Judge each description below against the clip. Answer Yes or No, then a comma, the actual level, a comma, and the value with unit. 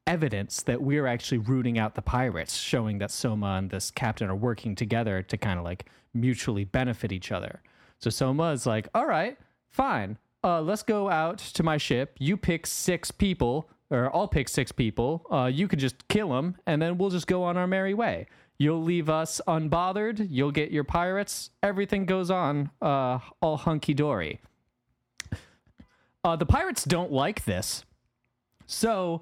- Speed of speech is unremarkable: Yes, average, 175 wpm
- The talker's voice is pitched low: No, medium, 145 Hz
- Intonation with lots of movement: Yes, wide, 6.5 semitones